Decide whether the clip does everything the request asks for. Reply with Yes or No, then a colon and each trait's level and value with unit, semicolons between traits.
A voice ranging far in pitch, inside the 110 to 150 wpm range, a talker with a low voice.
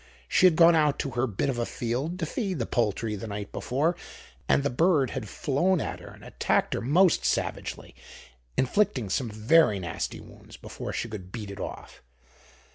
No: wide, 7.0 semitones; average, 190 wpm; low, 130 Hz